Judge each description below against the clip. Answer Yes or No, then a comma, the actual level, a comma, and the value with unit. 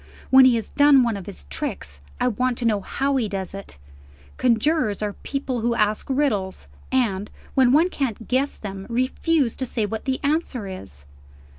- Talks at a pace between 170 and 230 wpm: Yes, average, 180 wpm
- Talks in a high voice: Yes, high, 235 Hz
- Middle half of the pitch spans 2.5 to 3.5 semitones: No, average, 4.7 semitones